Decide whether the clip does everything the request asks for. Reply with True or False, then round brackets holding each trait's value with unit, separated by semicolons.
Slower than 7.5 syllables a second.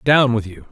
True (4.9 syllables/s)